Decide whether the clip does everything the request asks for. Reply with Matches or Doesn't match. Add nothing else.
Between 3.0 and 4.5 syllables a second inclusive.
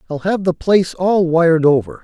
Doesn't match